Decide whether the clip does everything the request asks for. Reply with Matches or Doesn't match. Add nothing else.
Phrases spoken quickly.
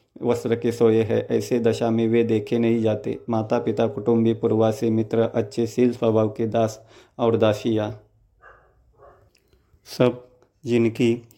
Doesn't match